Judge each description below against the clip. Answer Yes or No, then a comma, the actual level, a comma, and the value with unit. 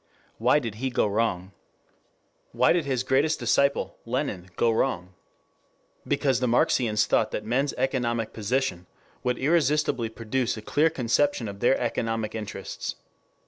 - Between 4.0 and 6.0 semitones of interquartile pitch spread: No, average, 3.2 semitones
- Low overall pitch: Yes, low, 120 Hz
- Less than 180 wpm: Yes, average, 140 wpm